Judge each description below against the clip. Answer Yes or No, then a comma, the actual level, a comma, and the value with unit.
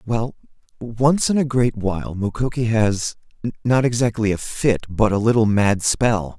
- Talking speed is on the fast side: No, average, 150 wpm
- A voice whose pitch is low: Yes, low, 115 Hz